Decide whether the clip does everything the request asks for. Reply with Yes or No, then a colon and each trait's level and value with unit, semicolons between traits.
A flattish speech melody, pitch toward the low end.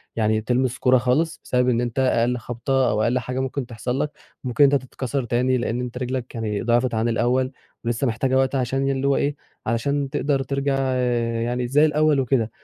Yes: narrow, 2.3 semitones; low, 125 Hz